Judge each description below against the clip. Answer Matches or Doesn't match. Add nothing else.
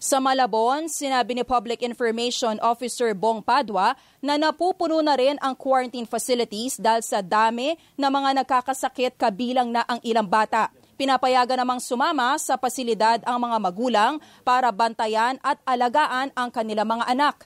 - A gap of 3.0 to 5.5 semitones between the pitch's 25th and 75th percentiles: Doesn't match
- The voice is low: Doesn't match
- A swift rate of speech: Doesn't match